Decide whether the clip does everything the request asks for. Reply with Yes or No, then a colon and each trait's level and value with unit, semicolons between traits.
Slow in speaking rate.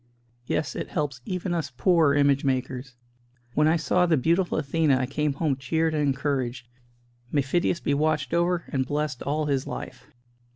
No: average, 170 wpm